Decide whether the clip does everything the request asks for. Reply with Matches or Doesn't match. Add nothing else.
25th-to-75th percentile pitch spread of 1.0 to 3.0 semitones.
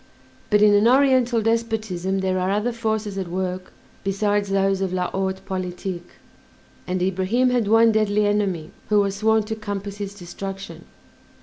Matches